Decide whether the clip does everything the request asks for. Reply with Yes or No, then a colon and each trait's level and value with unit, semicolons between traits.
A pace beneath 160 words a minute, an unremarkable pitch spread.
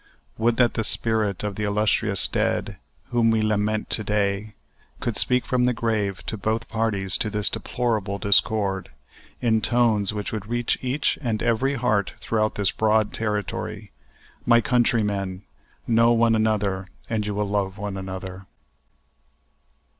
No: average, 145 wpm; narrow, 2.3 semitones